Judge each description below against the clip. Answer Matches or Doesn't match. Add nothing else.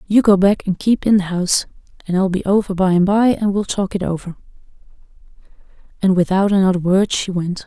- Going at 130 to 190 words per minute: Doesn't match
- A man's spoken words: Doesn't match